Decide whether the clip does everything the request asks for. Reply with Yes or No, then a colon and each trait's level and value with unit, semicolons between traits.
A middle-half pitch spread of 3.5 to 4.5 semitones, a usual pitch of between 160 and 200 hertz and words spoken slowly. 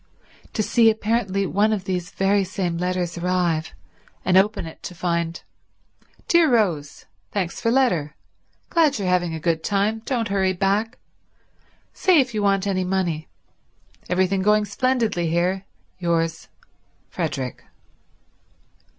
Yes: average, 3.8 semitones; high, 190 Hz; slow, 125 wpm